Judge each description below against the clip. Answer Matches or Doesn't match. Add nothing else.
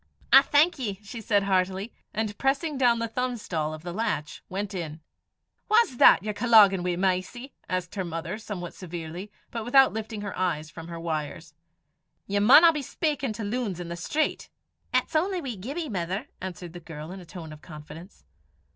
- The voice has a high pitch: Matches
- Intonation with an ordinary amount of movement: Doesn't match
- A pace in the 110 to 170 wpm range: Doesn't match